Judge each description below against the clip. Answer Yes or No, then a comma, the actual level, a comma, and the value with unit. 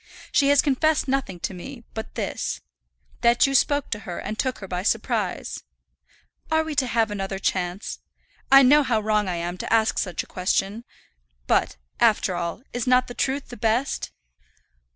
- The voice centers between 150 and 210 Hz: No, high, 230 Hz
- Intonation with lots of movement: Yes, wide, 5.8 semitones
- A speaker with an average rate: Yes, average, 175 wpm